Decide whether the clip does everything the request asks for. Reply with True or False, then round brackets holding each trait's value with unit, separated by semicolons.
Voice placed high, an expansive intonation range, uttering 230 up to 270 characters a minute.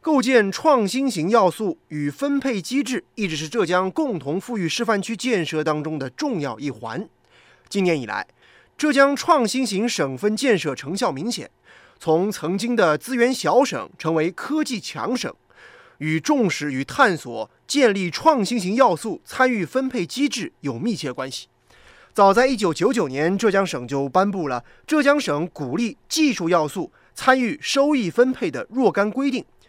True (220 Hz; 8.0 semitones; 240 characters per minute)